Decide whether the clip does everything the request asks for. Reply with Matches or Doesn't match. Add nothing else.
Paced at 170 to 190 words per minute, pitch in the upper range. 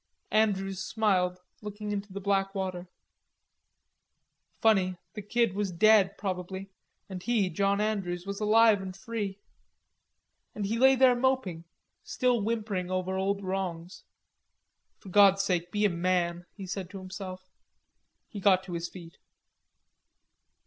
Doesn't match